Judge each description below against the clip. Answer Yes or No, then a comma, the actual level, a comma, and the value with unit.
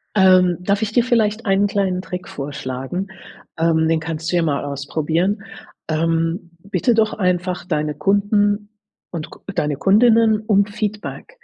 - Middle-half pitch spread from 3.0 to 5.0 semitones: Yes, average, 4.3 semitones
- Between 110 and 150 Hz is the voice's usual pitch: No, medium, 185 Hz